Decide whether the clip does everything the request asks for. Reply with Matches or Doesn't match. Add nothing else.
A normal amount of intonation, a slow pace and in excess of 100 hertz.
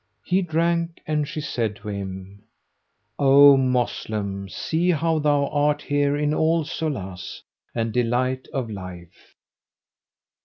Doesn't match